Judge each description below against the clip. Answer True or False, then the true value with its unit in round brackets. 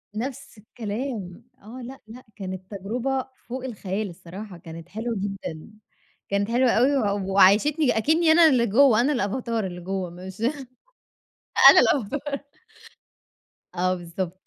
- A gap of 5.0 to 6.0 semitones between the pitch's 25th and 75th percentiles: True (5.3 semitones)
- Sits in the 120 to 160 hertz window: False (215 Hz)